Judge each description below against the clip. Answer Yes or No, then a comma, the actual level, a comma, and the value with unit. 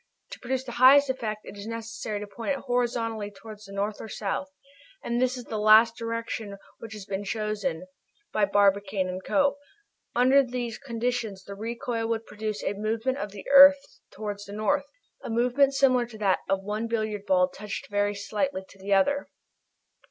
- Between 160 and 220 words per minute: Yes, average, 180 wpm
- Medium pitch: No, high, 220 Hz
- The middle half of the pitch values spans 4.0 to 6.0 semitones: No, average, 3.2 semitones